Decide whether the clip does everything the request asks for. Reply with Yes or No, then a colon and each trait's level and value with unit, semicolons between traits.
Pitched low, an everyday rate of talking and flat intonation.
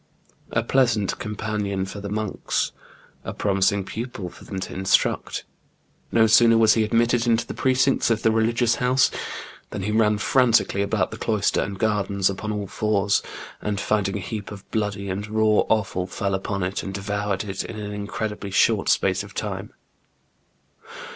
Yes: low, 105 Hz; average, 165 wpm; narrow, 2.1 semitones